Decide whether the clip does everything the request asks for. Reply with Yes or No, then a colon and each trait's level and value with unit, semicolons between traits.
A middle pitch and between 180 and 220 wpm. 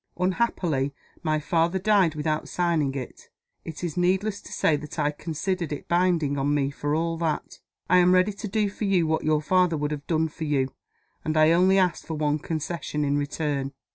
Yes: medium, 160 Hz; average, 200 wpm